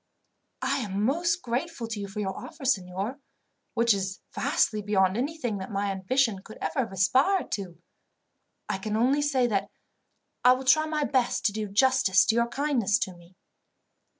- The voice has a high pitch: Yes, high, 230 Hz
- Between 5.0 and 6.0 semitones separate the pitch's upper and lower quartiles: Yes, average, 5.3 semitones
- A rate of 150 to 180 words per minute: Yes, average, 175 wpm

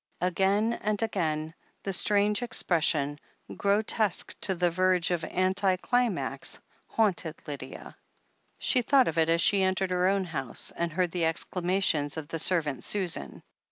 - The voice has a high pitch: No, medium, 180 Hz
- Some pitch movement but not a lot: Yes, average, 3.5 semitones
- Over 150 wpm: No, average, 145 wpm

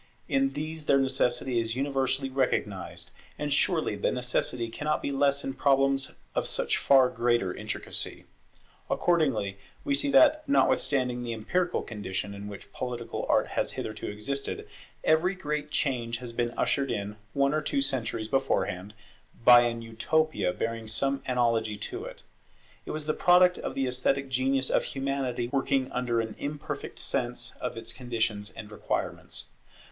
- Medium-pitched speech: No, low, 130 Hz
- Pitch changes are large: No, average, 3.3 semitones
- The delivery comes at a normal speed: Yes, average, 150 wpm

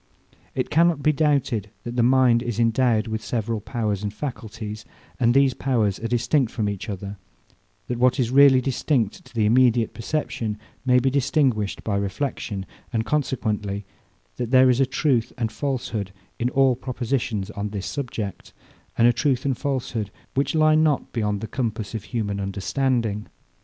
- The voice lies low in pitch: Yes, low, 120 Hz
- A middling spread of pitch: Yes, average, 3.7 semitones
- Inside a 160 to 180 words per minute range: Yes, average, 165 wpm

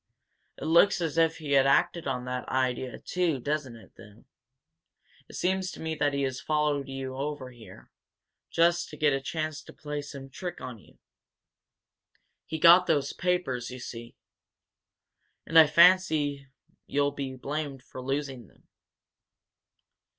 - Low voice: No, medium, 145 Hz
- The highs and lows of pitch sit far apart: No, average, 3.4 semitones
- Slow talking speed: No, average, 150 wpm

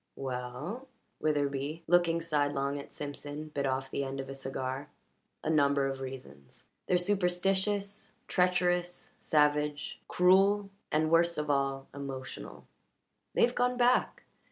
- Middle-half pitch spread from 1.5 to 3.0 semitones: No, average, 4.6 semitones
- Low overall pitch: No, medium, 150 Hz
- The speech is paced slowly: Yes, slow, 130 wpm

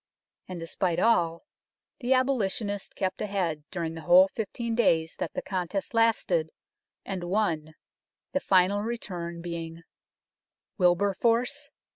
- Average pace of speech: No, slow, 115 wpm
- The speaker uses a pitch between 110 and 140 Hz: No, medium, 185 Hz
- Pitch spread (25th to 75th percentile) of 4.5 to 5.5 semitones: Yes, average, 4.8 semitones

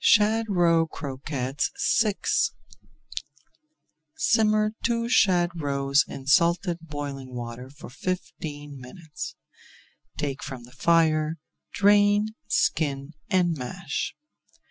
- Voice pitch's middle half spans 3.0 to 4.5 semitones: No, wide, 5.6 semitones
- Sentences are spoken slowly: Yes, slow, 95 wpm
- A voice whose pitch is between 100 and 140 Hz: No, medium, 160 Hz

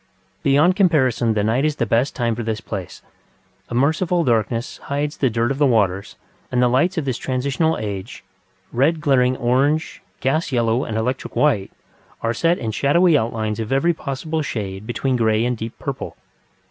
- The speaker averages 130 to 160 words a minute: No, average, 175 wpm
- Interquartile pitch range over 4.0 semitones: Yes, average, 4.4 semitones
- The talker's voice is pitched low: Yes, low, 125 Hz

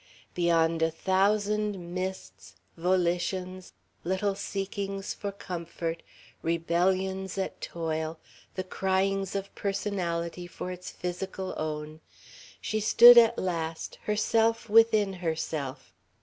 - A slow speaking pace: Yes, slow, 100 wpm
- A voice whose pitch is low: No, medium, 185 Hz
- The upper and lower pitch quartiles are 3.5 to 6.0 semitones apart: No, average, 2.8 semitones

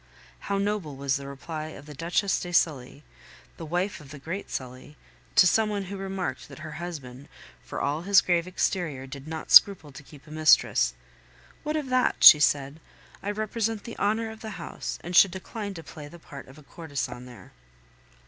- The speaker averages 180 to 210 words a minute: Yes, average, 195 wpm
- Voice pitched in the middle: Yes, medium, 165 Hz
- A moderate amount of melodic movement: No, wide, 5.7 semitones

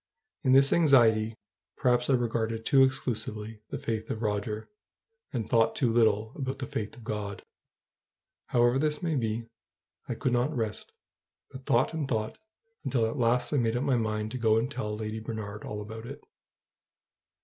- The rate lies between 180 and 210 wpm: No, average, 170 wpm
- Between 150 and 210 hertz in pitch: No, low, 115 Hz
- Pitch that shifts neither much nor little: Yes, average, 3.0 semitones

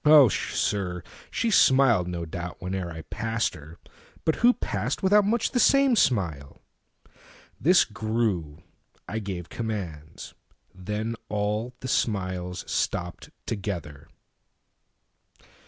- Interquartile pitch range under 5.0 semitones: No, wide, 5.4 semitones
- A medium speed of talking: No, slow, 95 wpm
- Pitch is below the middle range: Yes, low, 105 Hz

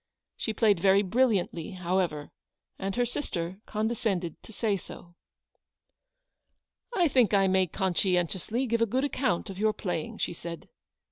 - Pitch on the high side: Yes, high, 195 Hz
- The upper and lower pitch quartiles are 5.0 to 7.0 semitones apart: No, average, 4.3 semitones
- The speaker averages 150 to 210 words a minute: No, average, 140 wpm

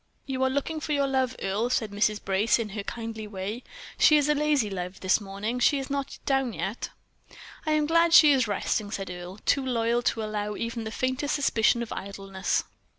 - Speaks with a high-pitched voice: Yes, high, 230 Hz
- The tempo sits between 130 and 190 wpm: No, fast, 205 wpm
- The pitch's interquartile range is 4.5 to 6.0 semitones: Yes, average, 5.0 semitones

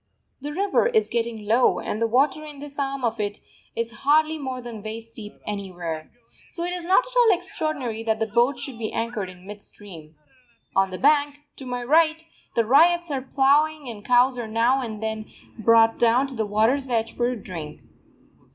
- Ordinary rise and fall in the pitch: Yes, average, 4.8 semitones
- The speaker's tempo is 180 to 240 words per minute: Yes, average, 195 wpm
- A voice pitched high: Yes, high, 240 Hz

